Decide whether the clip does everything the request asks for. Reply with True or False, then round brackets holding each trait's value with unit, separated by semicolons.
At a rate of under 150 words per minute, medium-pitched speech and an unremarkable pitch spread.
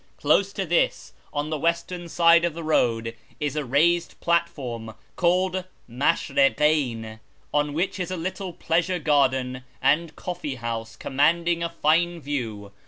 True (140 wpm; 155 Hz; 4.5 semitones)